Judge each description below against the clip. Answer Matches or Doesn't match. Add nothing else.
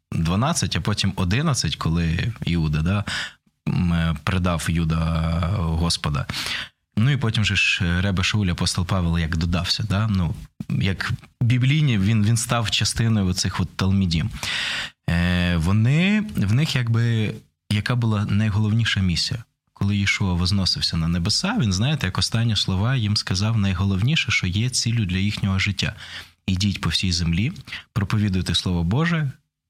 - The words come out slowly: Doesn't match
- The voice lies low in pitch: Matches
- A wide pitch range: Doesn't match